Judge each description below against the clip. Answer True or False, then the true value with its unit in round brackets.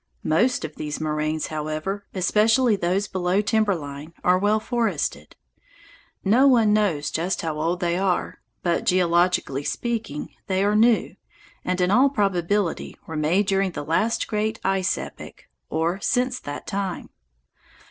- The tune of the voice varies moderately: True (4.5 semitones)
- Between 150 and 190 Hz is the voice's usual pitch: True (185 Hz)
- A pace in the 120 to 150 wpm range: True (145 wpm)